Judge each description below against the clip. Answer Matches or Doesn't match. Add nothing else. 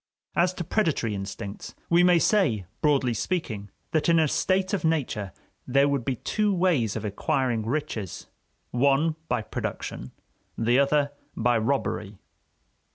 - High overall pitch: Doesn't match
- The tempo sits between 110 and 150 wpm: Matches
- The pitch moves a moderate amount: Doesn't match